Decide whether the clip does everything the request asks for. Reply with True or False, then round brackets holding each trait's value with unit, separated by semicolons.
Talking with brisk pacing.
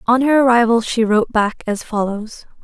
False (180 wpm)